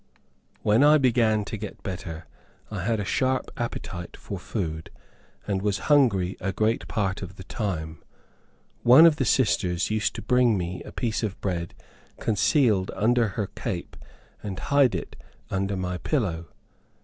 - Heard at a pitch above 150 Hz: No, low, 105 Hz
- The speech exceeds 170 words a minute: No, average, 155 wpm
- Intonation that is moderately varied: Yes, average, 4.3 semitones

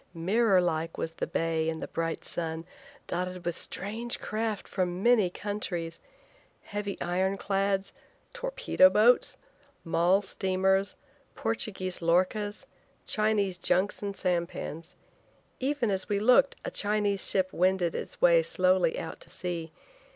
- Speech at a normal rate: No, slow, 130 wpm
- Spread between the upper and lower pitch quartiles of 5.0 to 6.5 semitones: No, average, 3.1 semitones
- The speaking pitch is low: No, high, 190 Hz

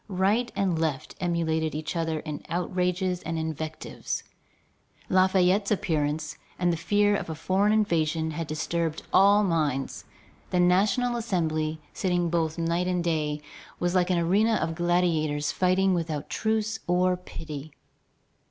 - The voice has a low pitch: No, medium, 175 Hz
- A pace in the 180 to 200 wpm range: No, slow, 135 wpm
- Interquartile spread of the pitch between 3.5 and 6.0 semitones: No, average, 2.9 semitones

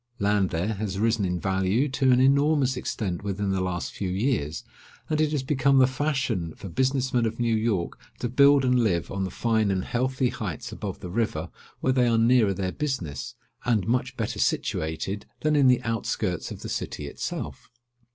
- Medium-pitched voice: No, low, 115 Hz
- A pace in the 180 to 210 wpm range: Yes, average, 190 wpm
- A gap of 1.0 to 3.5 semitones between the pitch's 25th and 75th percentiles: No, average, 5.3 semitones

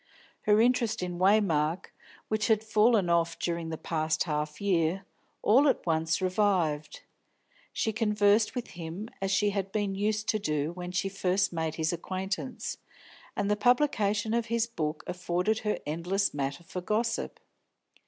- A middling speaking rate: Yes, average, 155 wpm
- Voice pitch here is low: No, high, 195 Hz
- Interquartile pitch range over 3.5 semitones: Yes, average, 4.4 semitones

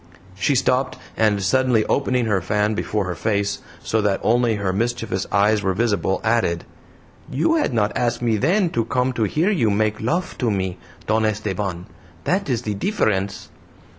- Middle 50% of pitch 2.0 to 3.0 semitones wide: No, average, 3.4 semitones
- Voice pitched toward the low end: Yes, low, 110 Hz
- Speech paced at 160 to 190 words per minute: Yes, average, 170 wpm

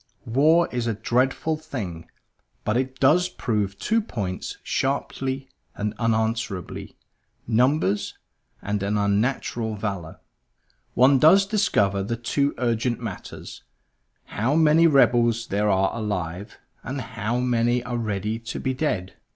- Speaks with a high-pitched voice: No, low, 115 Hz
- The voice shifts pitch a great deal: No, average, 4.3 semitones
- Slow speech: Yes, slow, 125 wpm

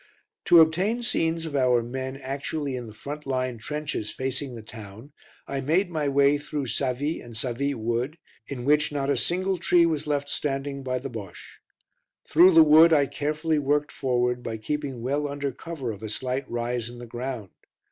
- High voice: No, medium, 140 Hz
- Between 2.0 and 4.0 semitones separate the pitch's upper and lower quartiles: Yes, average, 3.5 semitones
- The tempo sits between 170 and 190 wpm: Yes, average, 185 wpm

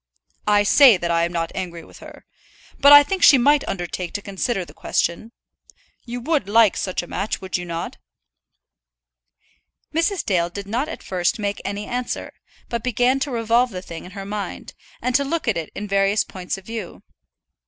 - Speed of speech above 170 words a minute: Yes, average, 190 wpm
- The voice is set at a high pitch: Yes, high, 205 Hz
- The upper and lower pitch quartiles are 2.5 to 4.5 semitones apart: No, average, 5.3 semitones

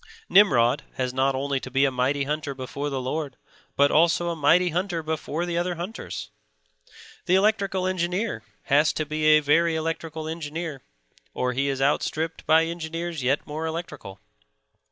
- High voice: No, medium, 155 Hz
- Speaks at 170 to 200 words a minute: No, average, 160 wpm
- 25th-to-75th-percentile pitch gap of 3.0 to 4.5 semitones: Yes, average, 3.5 semitones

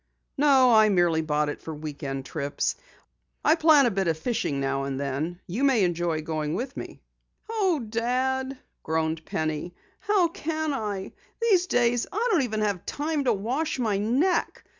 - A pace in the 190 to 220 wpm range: No, average, 175 wpm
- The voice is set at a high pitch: Yes, high, 215 Hz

